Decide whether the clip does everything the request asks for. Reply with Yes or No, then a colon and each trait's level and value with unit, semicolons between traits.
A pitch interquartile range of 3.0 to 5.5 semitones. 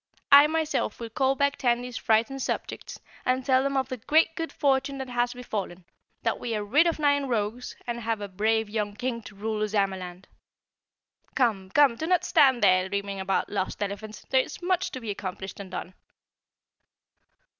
Yes: average, 4.9 semitones